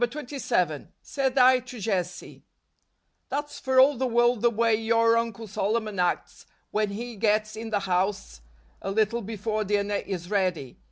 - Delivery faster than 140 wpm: Yes, average, 165 wpm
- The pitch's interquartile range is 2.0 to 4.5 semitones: Yes, average, 3.2 semitones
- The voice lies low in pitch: No, high, 220 Hz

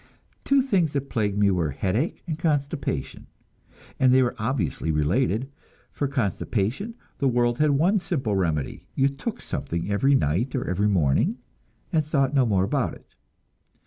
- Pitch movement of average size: No, wide, 6.7 semitones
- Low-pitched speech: Yes, low, 125 Hz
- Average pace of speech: Yes, average, 155 wpm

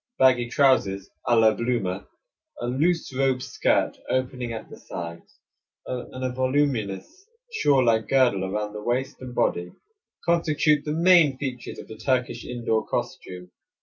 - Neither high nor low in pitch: No, low, 125 Hz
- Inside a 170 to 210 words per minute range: No, average, 145 wpm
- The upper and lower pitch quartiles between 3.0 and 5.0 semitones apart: Yes, average, 3.6 semitones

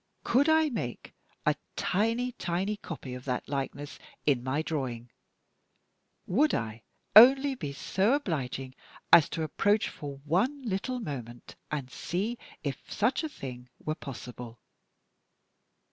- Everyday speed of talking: No, slow, 130 wpm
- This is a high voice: No, medium, 160 Hz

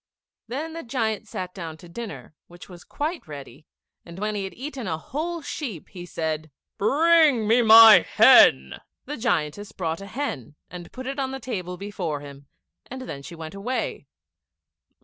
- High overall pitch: Yes, high, 205 Hz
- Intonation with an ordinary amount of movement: No, wide, 7.8 semitones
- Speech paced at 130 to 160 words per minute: No, average, 170 wpm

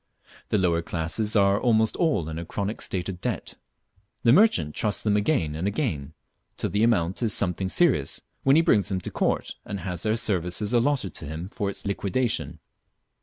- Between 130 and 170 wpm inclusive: No, average, 185 wpm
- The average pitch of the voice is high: No, low, 100 Hz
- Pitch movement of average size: Yes, average, 4.6 semitones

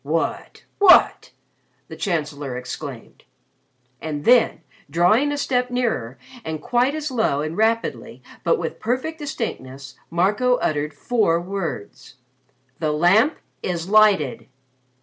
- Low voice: No, high, 195 Hz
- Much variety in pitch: Yes, wide, 8.4 semitones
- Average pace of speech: No, slow, 115 wpm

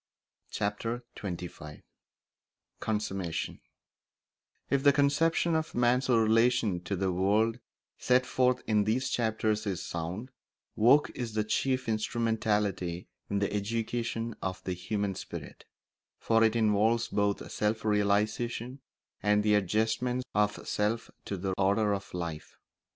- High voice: No, low, 110 Hz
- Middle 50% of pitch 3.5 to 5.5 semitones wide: No, average, 2.8 semitones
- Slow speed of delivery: Yes, slow, 125 wpm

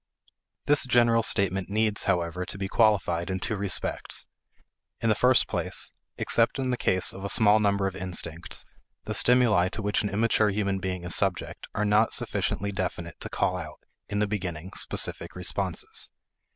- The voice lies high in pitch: No, low, 100 Hz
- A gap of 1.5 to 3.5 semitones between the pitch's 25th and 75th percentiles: Yes, average, 2.8 semitones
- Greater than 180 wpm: No, average, 170 wpm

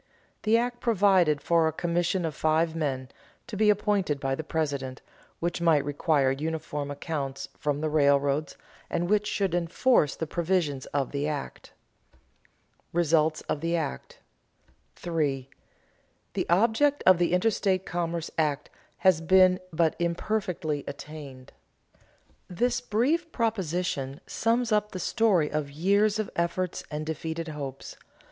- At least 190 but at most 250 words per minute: No, slow, 135 wpm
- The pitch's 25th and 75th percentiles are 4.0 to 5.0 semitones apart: Yes, average, 4.4 semitones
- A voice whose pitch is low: No, medium, 165 Hz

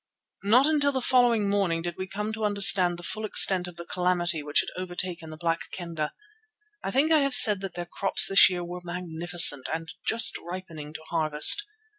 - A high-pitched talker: No, medium, 180 Hz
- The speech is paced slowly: No, average, 195 wpm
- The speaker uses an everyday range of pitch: Yes, average, 3.6 semitones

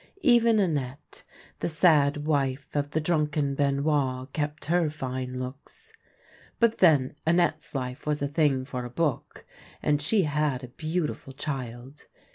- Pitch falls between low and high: Yes, medium, 145 Hz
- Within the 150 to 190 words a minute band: No, average, 140 wpm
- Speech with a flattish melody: No, average, 3.1 semitones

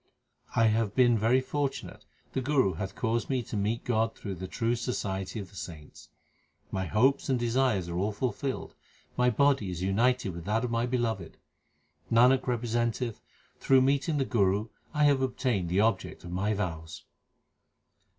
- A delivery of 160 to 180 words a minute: Yes, average, 165 wpm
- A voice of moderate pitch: No, low, 115 Hz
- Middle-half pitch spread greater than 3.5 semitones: Yes, average, 4.7 semitones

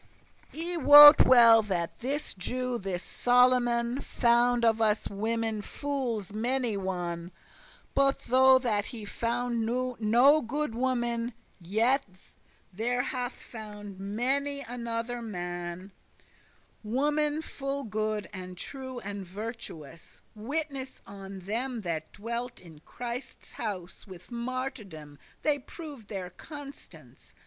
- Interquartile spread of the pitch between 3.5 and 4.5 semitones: Yes, average, 4.2 semitones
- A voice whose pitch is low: No, high, 235 Hz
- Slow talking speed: Yes, slow, 110 wpm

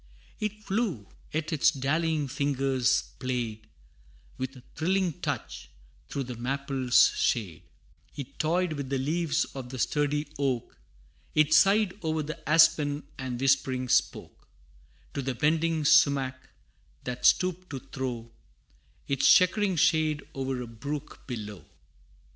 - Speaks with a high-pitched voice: No, medium, 140 Hz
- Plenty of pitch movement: No, average, 3.6 semitones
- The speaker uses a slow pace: Yes, slow, 125 wpm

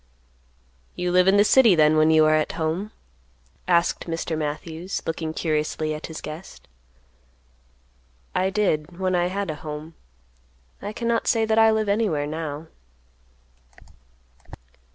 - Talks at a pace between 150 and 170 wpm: No, slow, 135 wpm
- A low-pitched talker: No, medium, 165 Hz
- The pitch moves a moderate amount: Yes, average, 4.2 semitones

